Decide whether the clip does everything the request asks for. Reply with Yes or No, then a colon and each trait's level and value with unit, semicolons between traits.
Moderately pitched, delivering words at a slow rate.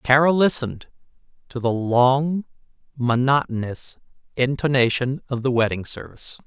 No: low, 130 Hz; slow, 100 wpm